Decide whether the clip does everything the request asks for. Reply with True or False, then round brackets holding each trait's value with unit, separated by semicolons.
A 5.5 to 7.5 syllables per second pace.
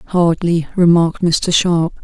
False (3.8 syllables/s)